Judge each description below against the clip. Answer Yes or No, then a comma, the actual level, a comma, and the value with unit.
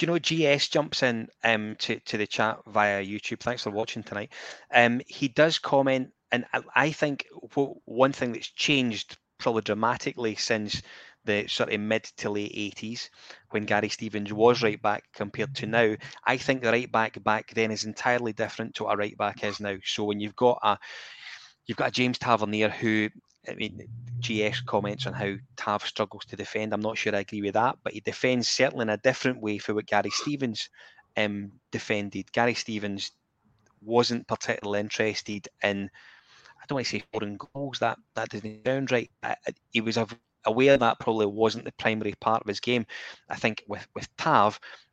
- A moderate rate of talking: Yes, average, 190 wpm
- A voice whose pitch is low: Yes, low, 110 Hz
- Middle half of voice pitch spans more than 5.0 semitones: No, average, 2.8 semitones